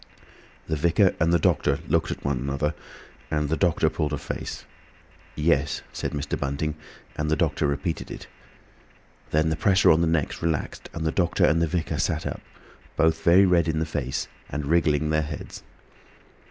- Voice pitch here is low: Yes, very low, 80 Hz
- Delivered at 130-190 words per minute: Yes, average, 180 wpm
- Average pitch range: No, narrow, 2.0 semitones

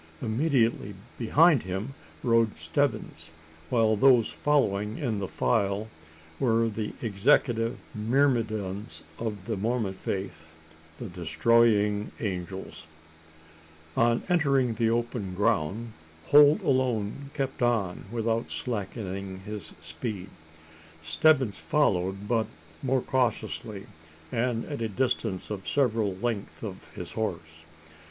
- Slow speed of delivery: Yes, slow, 105 wpm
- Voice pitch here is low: Yes, low, 110 Hz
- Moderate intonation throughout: Yes, average, 3.7 semitones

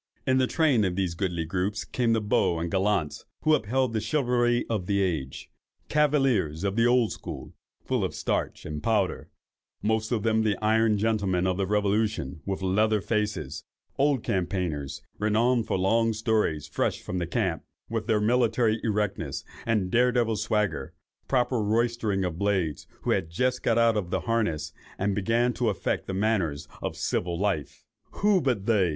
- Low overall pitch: Yes, low, 105 Hz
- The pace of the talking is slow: No, average, 165 wpm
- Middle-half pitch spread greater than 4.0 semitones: No, average, 3.7 semitones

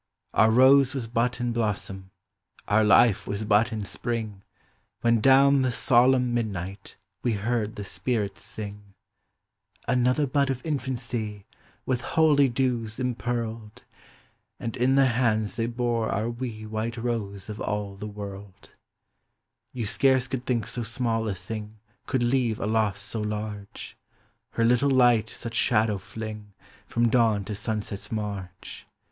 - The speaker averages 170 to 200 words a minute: No, average, 150 wpm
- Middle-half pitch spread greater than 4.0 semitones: No, average, 2.9 semitones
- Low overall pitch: Yes, low, 115 Hz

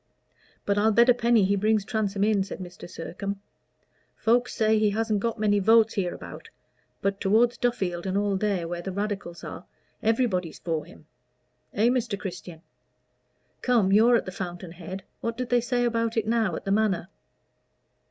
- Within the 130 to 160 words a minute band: No, average, 170 wpm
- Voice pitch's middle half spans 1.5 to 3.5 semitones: Yes, average, 3.2 semitones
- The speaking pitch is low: No, high, 205 Hz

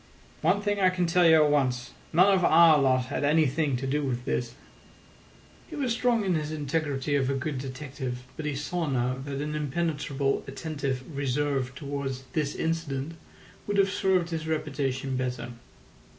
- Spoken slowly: No, average, 170 wpm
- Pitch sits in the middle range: Yes, medium, 145 Hz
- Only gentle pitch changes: No, average, 3.5 semitones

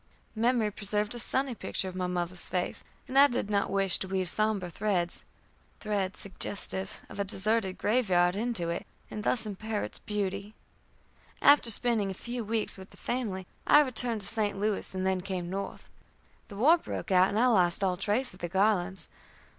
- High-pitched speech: Yes, high, 200 Hz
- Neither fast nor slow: Yes, average, 185 wpm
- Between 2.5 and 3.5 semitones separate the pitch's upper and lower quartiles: Yes, average, 3.0 semitones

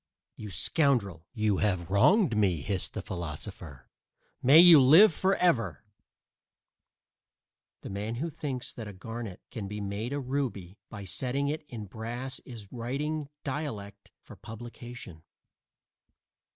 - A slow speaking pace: Yes, slow, 125 wpm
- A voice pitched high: No, low, 115 Hz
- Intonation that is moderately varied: No, wide, 5.7 semitones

